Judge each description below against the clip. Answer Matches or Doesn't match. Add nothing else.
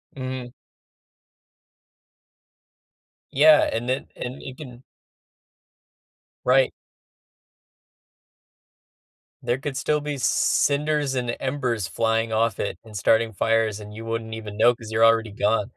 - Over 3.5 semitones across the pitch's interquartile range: Doesn't match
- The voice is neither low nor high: Doesn't match